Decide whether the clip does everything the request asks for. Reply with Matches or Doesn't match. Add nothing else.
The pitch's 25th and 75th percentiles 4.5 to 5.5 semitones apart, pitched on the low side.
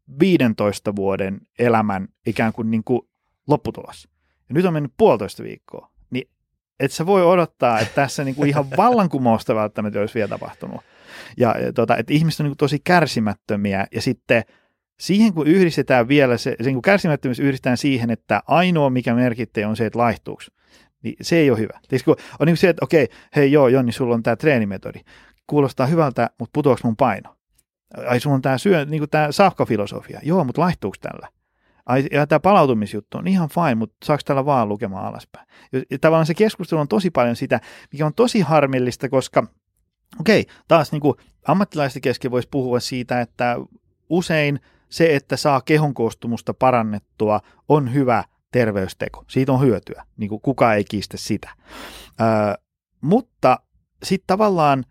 Matches